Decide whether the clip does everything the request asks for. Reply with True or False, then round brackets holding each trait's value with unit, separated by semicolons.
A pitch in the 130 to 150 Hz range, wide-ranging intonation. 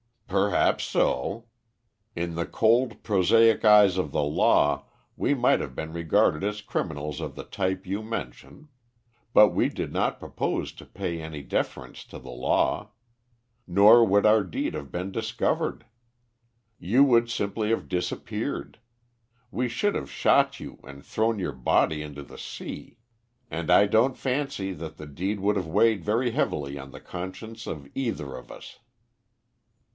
False (95 Hz; 6.0 semitones)